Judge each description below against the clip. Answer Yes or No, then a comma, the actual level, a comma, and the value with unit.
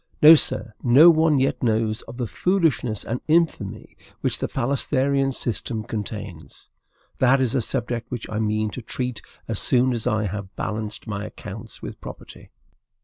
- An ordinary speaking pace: Yes, average, 160 wpm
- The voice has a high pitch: No, low, 120 Hz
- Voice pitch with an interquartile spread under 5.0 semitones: Yes, average, 3.8 semitones